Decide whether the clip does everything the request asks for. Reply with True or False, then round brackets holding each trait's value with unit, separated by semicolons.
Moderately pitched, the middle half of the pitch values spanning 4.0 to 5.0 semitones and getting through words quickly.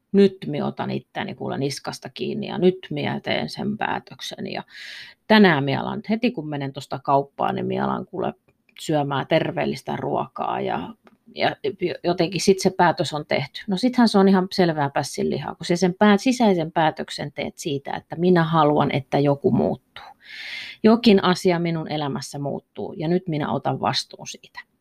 True (180 Hz; 4.7 semitones; 160 wpm)